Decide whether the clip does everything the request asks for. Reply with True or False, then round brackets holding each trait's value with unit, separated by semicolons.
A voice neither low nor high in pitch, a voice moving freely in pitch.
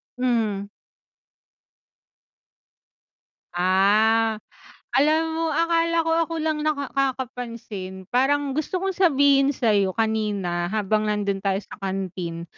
False (225 Hz; 6.4 semitones)